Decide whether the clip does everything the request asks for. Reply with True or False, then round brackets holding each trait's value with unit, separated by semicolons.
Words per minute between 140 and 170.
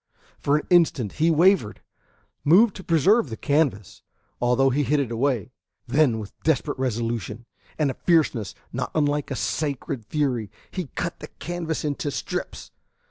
True (150 wpm)